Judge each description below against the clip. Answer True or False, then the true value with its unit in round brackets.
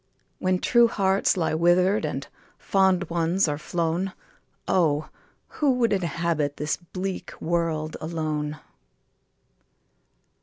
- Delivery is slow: True (105 wpm)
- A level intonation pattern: False (3.3 semitones)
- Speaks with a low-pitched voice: False (170 Hz)